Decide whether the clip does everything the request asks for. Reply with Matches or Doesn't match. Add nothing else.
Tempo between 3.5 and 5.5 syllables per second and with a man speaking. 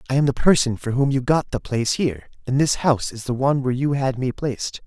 Doesn't match